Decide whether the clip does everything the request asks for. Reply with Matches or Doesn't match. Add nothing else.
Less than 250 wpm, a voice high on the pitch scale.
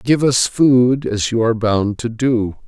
Doesn't match